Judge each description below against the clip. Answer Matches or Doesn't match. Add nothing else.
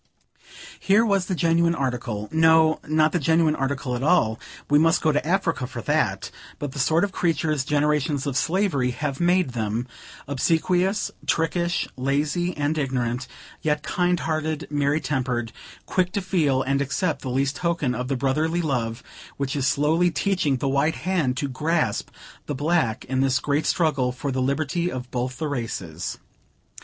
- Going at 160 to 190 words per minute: Matches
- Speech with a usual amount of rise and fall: Matches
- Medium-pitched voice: Matches